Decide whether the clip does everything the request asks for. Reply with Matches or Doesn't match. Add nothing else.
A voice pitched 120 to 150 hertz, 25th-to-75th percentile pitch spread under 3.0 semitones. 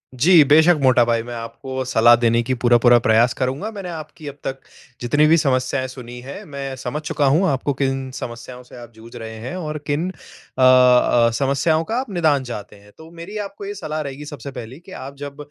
Doesn't match